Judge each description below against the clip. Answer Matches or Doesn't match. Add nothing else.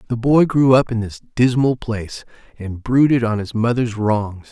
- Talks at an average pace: Matches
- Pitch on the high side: Doesn't match